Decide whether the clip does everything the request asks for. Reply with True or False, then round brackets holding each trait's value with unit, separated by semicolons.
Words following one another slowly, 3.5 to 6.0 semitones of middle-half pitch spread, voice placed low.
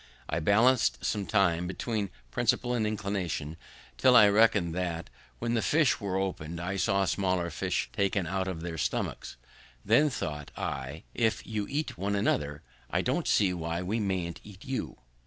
False (165 wpm; 4.0 semitones; 95 Hz)